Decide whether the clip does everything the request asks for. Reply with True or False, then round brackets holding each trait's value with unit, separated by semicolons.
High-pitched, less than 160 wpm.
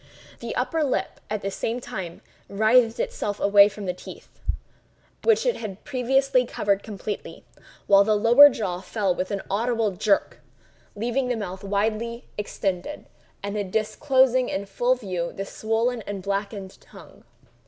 True (210 Hz; 145 wpm)